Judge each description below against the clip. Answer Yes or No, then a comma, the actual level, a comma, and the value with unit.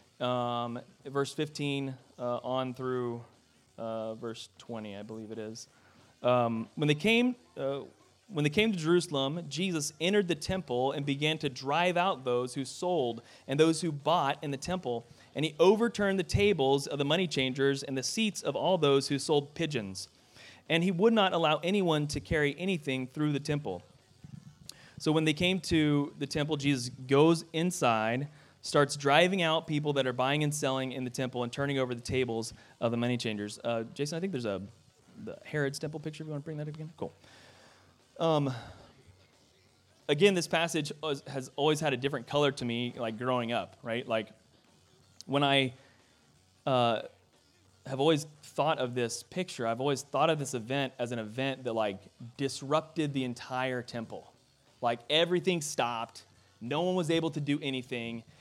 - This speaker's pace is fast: No, average, 180 wpm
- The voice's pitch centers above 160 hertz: No, medium, 140 Hz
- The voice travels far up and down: No, average, 4.4 semitones